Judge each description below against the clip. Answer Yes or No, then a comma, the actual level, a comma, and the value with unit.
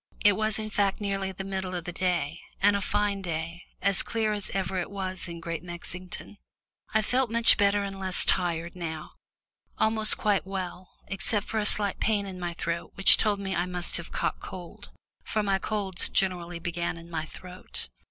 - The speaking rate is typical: Yes, average, 190 wpm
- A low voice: No, high, 190 Hz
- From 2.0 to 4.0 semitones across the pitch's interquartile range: Yes, average, 2.7 semitones